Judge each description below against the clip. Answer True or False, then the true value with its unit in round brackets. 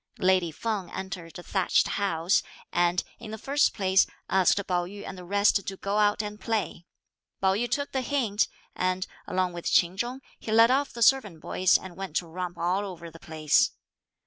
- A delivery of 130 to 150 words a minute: False (195 wpm)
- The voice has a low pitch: False (190 Hz)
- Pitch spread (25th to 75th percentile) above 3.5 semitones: False (3.2 semitones)